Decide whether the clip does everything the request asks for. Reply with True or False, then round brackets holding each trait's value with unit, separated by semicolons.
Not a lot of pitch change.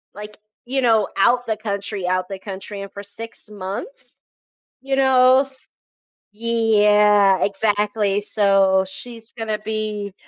True (2.3 semitones)